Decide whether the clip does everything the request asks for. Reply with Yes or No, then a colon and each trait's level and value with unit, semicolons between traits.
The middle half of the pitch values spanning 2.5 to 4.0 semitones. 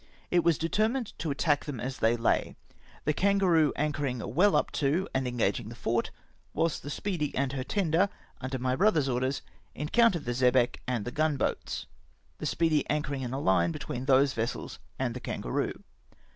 No: average, 4.5 semitones